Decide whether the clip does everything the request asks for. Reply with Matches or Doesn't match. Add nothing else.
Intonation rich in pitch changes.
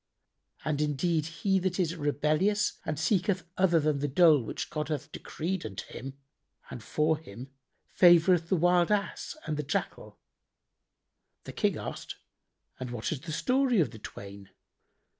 Doesn't match